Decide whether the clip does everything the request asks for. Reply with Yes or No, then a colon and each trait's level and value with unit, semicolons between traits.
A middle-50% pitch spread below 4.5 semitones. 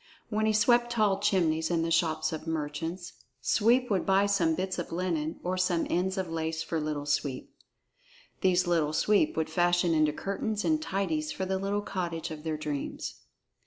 Yes: average, 3.6 semitones